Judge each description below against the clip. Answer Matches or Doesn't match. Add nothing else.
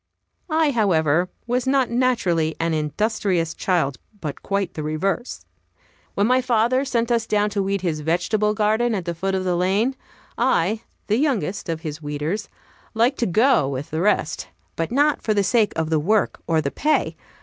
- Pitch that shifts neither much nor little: Doesn't match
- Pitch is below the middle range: Doesn't match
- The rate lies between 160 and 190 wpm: Matches